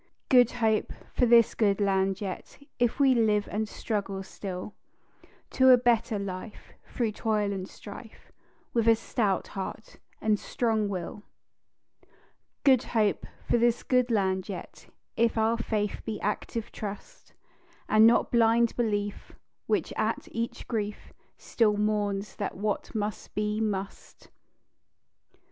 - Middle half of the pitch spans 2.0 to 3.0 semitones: Yes, narrow, 2.4 semitones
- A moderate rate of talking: No, slow, 130 wpm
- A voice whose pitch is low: No, high, 215 Hz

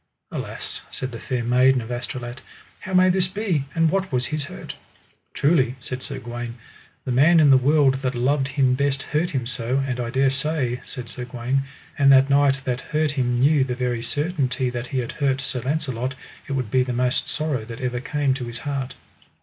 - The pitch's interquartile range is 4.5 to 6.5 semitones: No, narrow, 2.5 semitones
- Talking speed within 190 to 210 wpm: Yes, fast, 205 wpm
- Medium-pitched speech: No, low, 130 Hz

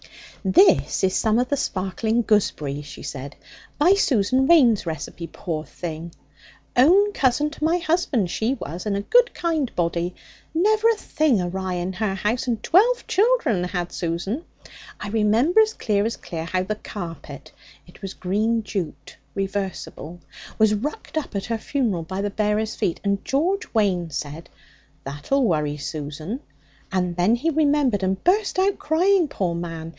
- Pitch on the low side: No, high, 205 Hz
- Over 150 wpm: Yes, average, 160 wpm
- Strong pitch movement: Yes, wide, 8.1 semitones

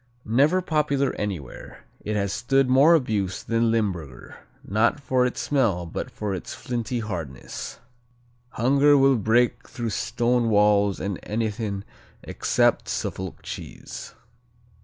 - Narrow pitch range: No, average, 4.4 semitones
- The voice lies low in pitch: Yes, low, 115 Hz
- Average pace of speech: No, slow, 125 wpm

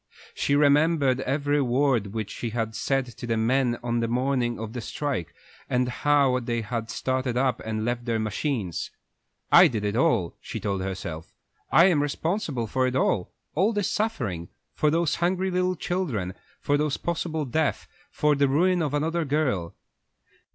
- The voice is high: No, low, 130 Hz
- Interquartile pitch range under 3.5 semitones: No, average, 4.9 semitones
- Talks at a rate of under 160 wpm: No, average, 170 wpm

